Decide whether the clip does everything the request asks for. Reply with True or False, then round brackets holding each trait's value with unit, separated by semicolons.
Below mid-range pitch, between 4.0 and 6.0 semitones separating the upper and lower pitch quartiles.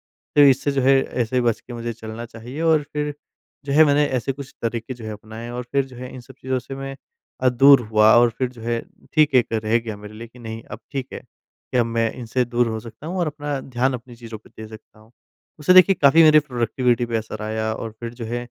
False (120 Hz; 3.1 semitones)